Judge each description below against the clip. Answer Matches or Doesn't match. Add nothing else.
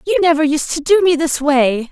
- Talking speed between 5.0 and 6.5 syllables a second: Matches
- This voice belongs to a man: Doesn't match